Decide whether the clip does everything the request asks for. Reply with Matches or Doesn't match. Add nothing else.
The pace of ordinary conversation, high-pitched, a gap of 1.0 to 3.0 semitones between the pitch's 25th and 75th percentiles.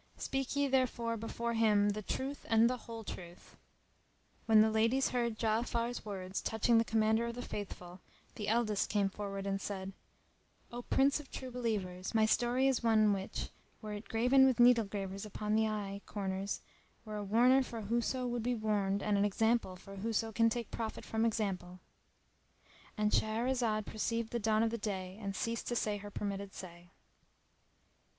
Matches